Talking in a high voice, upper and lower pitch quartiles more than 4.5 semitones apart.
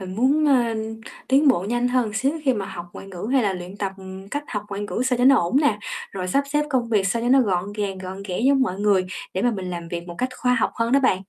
Yes: high, 210 Hz; average, 5.1 semitones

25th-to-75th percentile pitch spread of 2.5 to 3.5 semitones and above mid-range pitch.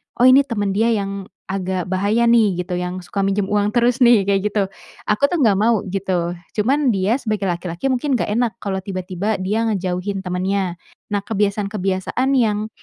Yes: average, 3.1 semitones; high, 200 Hz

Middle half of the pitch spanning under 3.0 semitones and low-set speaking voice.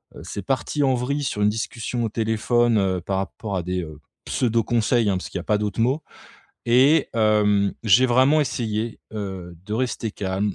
No: average, 3.5 semitones; low, 110 Hz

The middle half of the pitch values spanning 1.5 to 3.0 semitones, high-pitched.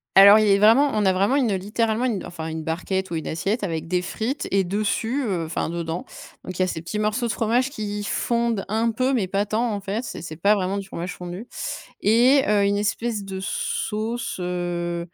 No: average, 3.7 semitones; high, 205 Hz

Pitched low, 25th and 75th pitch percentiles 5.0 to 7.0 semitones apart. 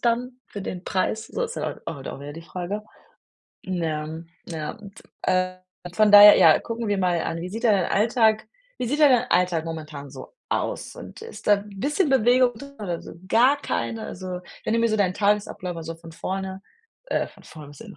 No: high, 195 Hz; wide, 5.5 semitones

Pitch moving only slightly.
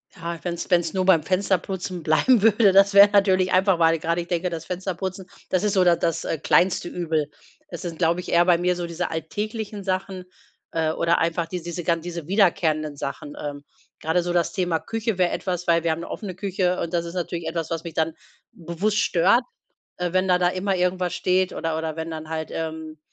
Yes: narrow, 2.3 semitones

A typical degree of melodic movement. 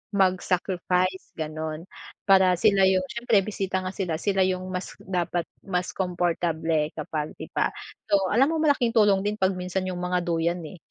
No: narrow, 1.9 semitones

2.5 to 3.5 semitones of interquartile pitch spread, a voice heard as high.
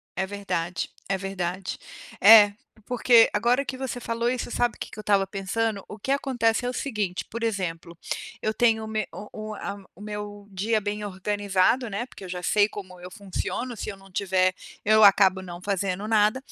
Yes: average, 2.9 semitones; high, 205 Hz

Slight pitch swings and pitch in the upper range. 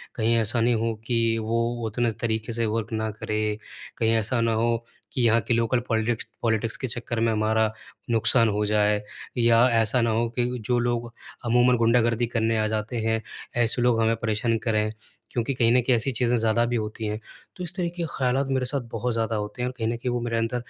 No: narrow, 1.4 semitones; low, 115 Hz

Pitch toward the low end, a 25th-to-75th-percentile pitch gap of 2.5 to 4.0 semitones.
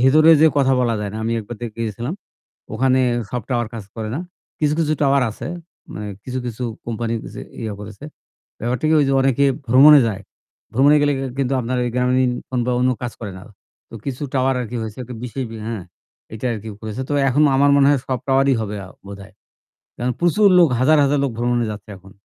Yes: low, 125 Hz; average, 3.5 semitones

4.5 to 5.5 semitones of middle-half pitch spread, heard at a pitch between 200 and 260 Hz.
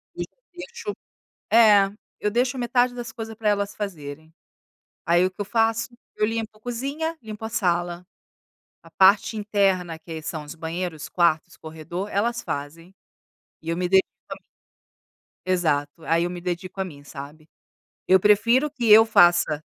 No: average, 5.1 semitones; high, 190 Hz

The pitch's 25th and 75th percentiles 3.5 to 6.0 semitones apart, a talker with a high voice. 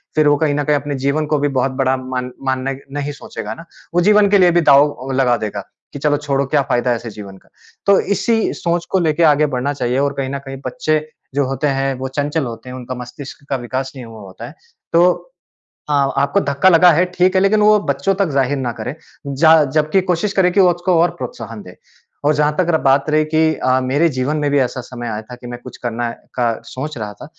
No: average, 3.9 semitones; medium, 140 Hz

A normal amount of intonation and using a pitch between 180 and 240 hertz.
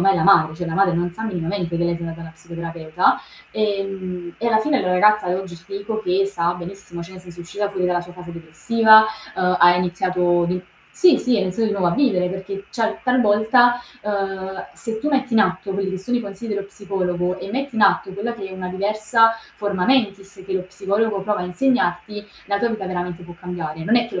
Yes: average, 3.2 semitones; high, 190 Hz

